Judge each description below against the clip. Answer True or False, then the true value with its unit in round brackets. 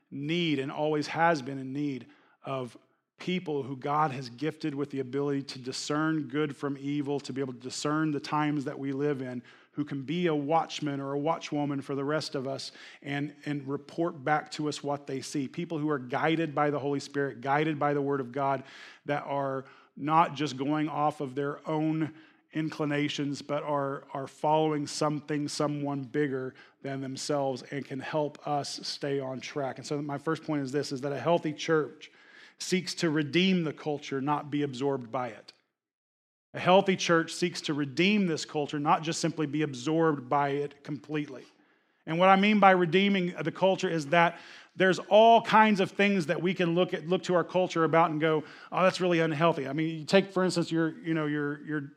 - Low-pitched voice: False (150 Hz)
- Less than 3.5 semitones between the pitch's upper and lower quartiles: True (2.6 semitones)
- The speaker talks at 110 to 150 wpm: False (200 wpm)